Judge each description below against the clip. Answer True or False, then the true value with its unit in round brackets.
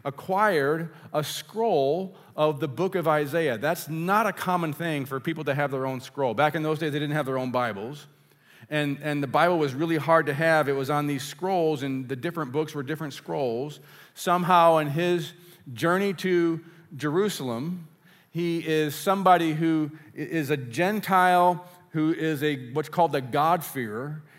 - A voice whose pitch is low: False (155 Hz)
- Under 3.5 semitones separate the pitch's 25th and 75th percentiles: True (2.7 semitones)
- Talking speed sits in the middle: True (175 wpm)